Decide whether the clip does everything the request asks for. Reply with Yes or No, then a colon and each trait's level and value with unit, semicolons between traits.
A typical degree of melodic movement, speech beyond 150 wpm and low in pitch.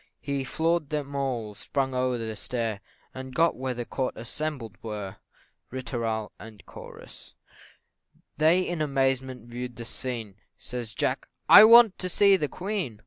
No: average, 4.8 semitones; average, 145 wpm; low, 130 Hz